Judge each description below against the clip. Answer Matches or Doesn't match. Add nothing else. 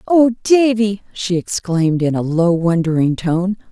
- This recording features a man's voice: Doesn't match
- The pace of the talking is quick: Doesn't match